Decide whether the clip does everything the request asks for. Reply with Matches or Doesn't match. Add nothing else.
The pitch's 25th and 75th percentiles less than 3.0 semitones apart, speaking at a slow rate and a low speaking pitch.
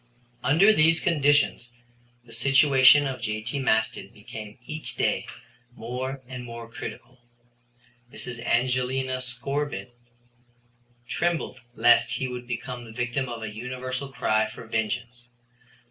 Matches